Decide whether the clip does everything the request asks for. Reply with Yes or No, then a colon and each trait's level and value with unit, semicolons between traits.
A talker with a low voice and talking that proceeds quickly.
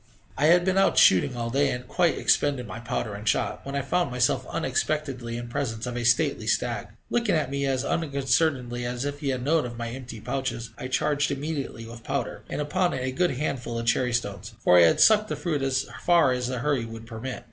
Yes: low, 130 Hz; fast, 225 wpm